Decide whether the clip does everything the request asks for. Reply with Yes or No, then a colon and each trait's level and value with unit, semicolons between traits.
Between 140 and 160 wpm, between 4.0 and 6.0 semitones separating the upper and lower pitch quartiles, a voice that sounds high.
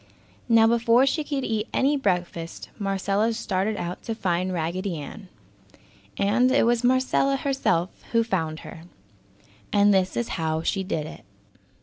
Yes: average, 145 wpm; average, 4.9 semitones; high, 205 Hz